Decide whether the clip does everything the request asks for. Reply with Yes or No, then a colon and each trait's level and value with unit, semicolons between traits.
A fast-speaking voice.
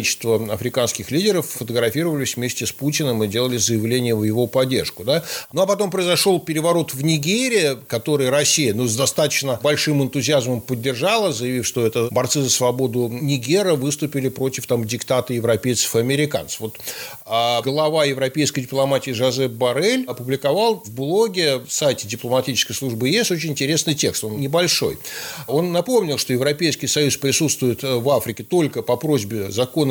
No: average, 150 wpm